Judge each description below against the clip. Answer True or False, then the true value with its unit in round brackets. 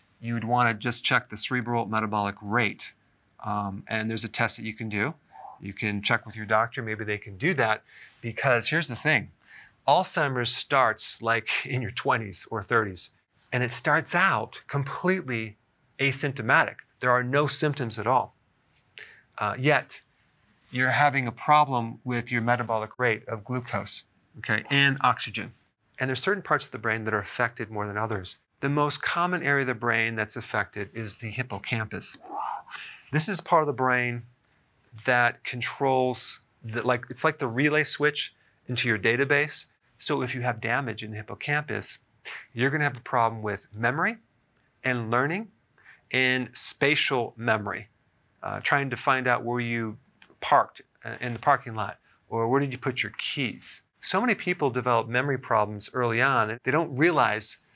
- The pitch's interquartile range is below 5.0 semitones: True (3.8 semitones)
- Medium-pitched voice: False (120 Hz)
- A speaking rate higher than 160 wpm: True (170 wpm)